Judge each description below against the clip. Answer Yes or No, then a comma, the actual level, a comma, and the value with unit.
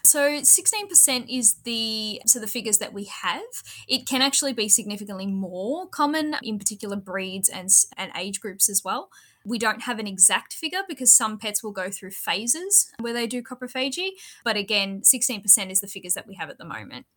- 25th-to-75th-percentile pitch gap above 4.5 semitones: Yes, average, 4.9 semitones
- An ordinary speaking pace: Yes, average, 190 wpm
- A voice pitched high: Yes, high, 225 Hz